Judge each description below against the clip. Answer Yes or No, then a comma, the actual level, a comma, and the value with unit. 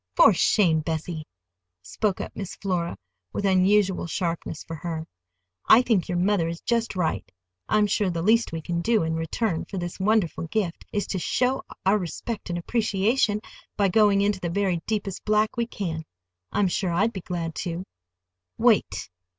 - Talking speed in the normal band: Yes, average, 170 wpm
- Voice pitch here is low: No, high, 190 Hz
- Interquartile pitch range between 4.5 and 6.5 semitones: No, average, 3.8 semitones